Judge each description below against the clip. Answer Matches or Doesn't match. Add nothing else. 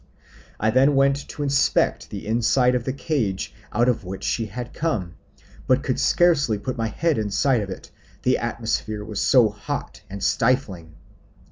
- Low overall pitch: Matches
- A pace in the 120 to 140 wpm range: Doesn't match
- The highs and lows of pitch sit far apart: Doesn't match